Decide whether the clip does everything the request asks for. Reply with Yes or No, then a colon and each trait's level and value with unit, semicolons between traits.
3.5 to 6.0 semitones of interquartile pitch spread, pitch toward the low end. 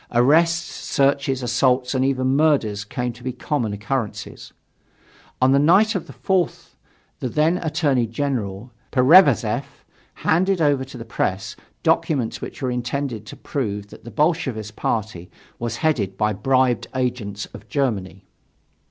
Yes: average, 4.5 semitones; low, 130 Hz